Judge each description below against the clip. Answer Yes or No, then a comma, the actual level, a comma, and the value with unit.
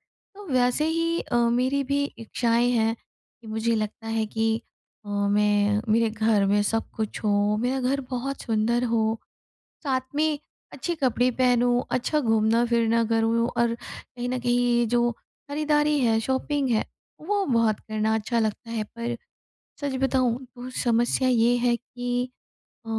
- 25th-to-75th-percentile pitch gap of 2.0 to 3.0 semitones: Yes, narrow, 2.4 semitones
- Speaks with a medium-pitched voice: No, high, 235 Hz